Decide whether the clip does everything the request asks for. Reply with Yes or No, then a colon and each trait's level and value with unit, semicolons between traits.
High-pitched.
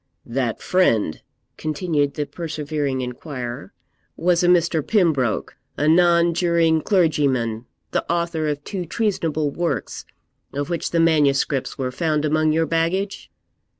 No: medium, 155 Hz